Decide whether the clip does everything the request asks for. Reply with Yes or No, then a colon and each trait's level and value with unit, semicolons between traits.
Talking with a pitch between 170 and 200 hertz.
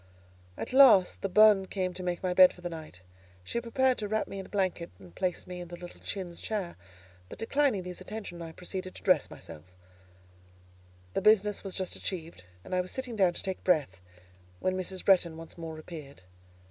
Yes: medium, 185 Hz